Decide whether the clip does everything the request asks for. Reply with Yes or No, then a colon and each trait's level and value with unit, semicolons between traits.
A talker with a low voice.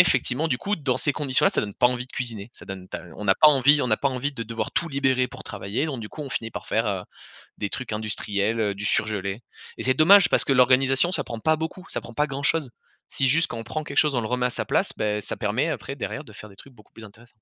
Yes: low, 125 Hz